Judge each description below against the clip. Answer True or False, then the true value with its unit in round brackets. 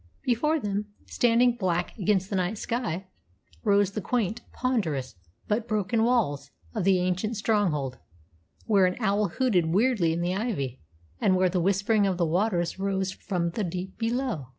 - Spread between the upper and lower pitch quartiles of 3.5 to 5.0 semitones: True (4.0 semitones)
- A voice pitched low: False (195 Hz)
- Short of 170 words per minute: True (160 wpm)